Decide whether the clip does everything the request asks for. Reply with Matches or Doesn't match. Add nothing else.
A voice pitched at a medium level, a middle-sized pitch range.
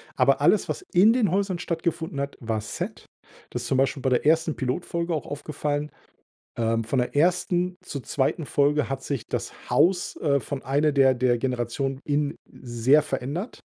Matches